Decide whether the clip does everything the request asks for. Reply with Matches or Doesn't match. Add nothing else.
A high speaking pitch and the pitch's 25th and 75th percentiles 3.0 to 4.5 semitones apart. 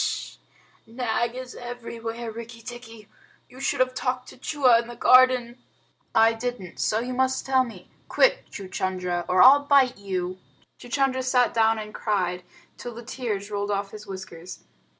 Matches